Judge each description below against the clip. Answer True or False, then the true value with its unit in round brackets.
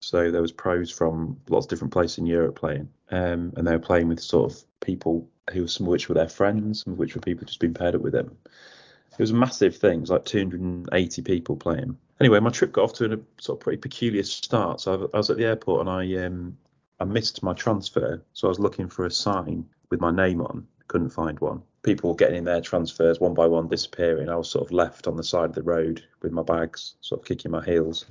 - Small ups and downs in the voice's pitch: True (2.2 semitones)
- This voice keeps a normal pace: False (250 wpm)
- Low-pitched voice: True (90 Hz)